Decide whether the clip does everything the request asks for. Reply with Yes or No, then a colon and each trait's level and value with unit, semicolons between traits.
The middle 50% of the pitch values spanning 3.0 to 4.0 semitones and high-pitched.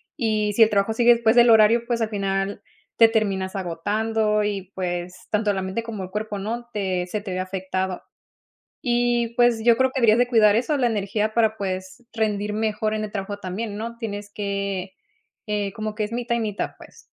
No: narrow, 2.6 semitones; high, 210 Hz